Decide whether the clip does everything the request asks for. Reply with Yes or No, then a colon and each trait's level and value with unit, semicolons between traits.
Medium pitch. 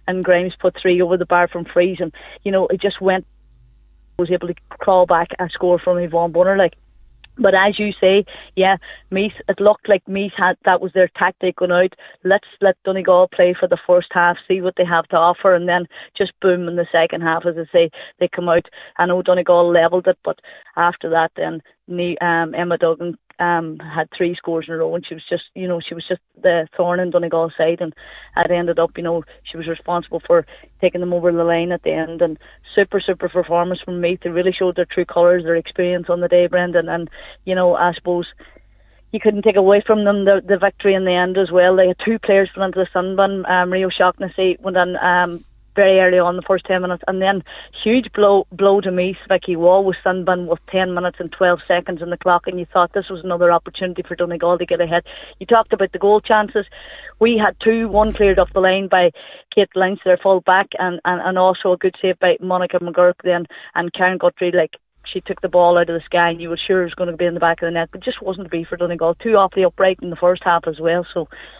Yes: medium, 180 Hz